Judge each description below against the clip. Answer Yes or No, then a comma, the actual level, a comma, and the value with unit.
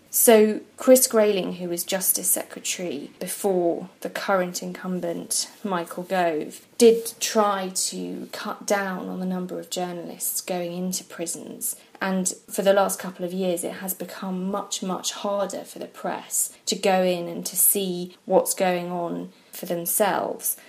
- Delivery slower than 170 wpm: Yes, average, 155 wpm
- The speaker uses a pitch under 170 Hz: No, medium, 185 Hz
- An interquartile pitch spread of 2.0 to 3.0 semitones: Yes, narrow, 2.6 semitones